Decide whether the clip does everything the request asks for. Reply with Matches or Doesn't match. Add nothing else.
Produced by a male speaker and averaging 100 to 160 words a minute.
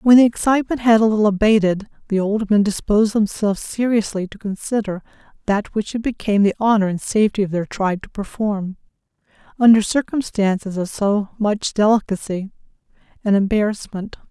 Doesn't match